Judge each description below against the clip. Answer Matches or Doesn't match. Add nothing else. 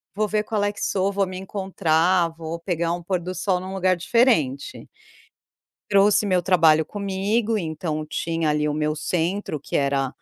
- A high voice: Doesn't match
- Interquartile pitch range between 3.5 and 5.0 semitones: Matches